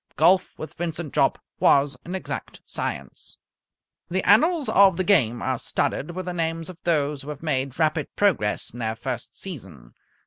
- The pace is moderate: Yes, average, 170 wpm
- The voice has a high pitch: No, medium, 160 Hz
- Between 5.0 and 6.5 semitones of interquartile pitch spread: Yes, average, 5.3 semitones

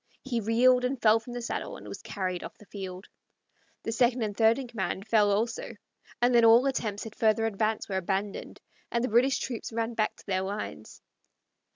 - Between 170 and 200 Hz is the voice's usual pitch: No, high, 225 Hz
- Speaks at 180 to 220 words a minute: Yes, average, 200 wpm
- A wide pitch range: No, average, 2.7 semitones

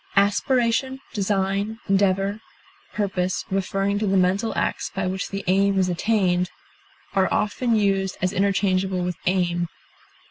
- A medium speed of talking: No, slow, 130 wpm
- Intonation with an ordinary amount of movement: No, narrow, 1.7 semitones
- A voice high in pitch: Yes, high, 195 Hz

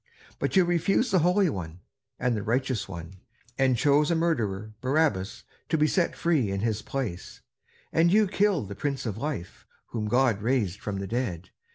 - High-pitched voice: No, low, 125 Hz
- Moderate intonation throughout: No, wide, 8.2 semitones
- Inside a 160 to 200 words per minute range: Yes, average, 180 wpm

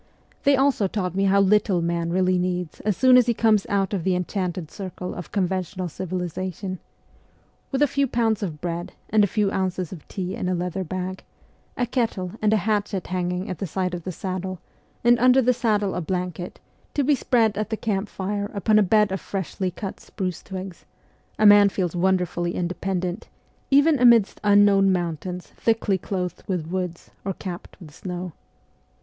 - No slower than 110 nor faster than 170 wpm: No, average, 185 wpm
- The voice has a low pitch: No, high, 190 Hz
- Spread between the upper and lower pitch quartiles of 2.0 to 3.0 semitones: Yes, average, 2.7 semitones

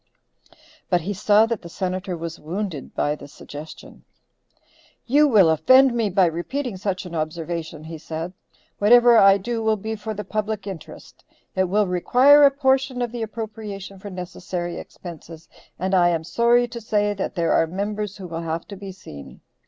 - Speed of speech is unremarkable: Yes, average, 175 wpm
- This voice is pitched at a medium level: No, high, 195 Hz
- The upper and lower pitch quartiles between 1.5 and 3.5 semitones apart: No, average, 4.4 semitones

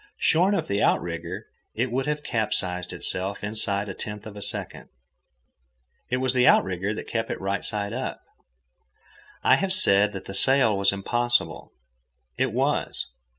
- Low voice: Yes, low, 105 Hz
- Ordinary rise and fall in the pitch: Yes, average, 4.1 semitones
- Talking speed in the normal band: Yes, average, 160 wpm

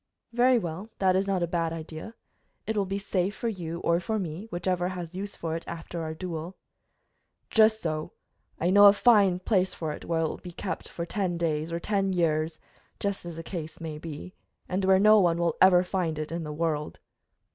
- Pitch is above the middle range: No, medium, 175 Hz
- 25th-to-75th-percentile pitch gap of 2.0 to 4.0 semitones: Yes, average, 3.0 semitones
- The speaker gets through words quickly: Yes, fast, 210 wpm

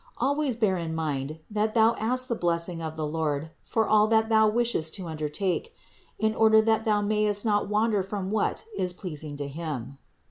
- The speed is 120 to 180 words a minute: No, average, 190 wpm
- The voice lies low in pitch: No, high, 205 Hz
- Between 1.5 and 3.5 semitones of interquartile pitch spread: No, wide, 5.5 semitones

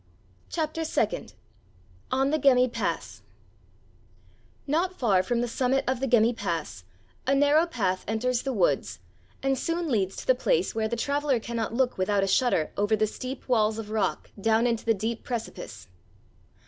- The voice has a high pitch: Yes, high, 240 Hz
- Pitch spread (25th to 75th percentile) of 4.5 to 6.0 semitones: No, average, 3.9 semitones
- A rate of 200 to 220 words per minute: No, average, 165 wpm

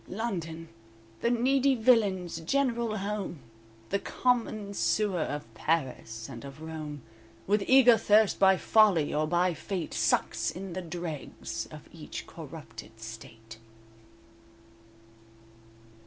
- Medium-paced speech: No, slow, 110 wpm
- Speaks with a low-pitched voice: No, medium, 185 Hz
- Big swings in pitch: Yes, wide, 5.8 semitones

